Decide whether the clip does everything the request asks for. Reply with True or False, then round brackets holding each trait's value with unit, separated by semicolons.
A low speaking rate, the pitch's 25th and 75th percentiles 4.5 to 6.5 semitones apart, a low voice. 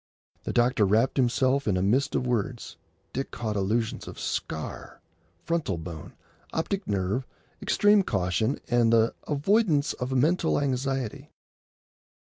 True (125 wpm; 5.1 semitones; 125 Hz)